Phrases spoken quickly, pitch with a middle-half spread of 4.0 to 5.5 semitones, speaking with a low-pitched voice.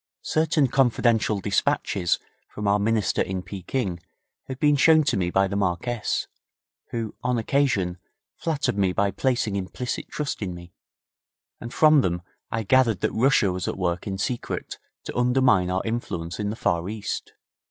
No: average, 160 wpm; average, 5.2 semitones; low, 105 Hz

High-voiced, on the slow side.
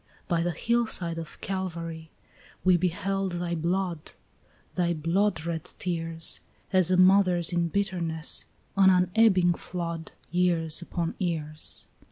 No: medium, 175 Hz; slow, 115 wpm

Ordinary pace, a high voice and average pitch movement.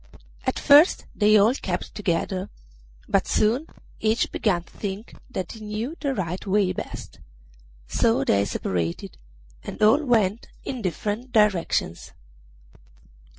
No: slow, 125 wpm; high, 210 Hz; average, 4.1 semitones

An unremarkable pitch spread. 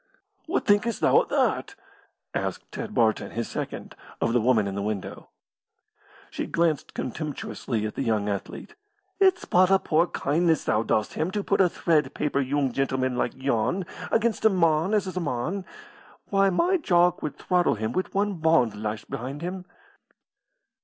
No: wide, 7.7 semitones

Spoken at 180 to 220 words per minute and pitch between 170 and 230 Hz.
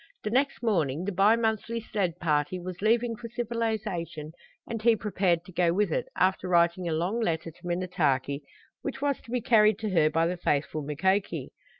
Yes: average, 190 wpm; medium, 185 Hz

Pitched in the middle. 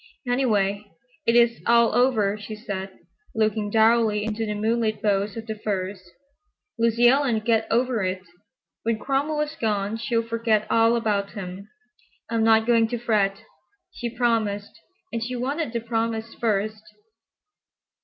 No: high, 225 Hz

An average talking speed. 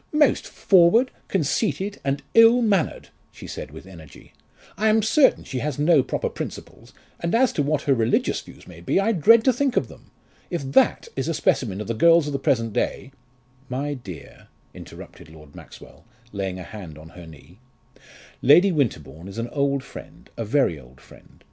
Yes: average, 185 wpm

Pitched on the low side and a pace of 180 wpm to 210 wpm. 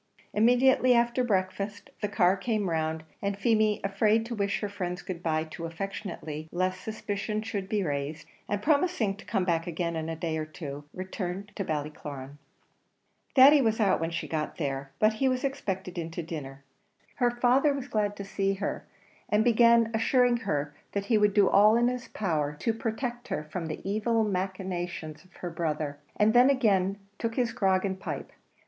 No: high, 195 Hz; average, 185 wpm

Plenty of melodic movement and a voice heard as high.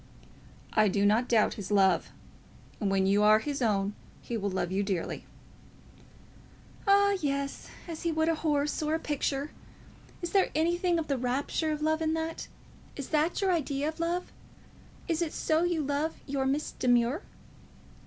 Yes: wide, 6.0 semitones; very high, 290 Hz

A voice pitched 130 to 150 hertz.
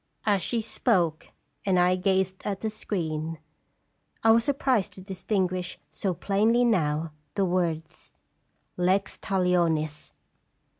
No: medium, 185 Hz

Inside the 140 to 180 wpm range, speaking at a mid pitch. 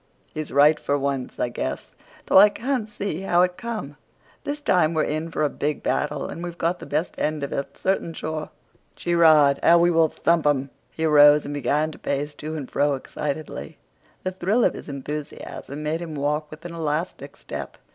No: average, 200 wpm; medium, 155 Hz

